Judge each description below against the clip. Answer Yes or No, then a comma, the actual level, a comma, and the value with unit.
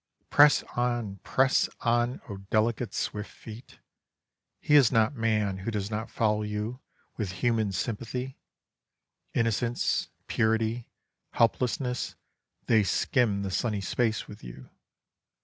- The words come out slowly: Yes, slow, 115 wpm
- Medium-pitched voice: No, low, 115 Hz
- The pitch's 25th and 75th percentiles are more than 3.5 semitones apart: No, narrow, 2.5 semitones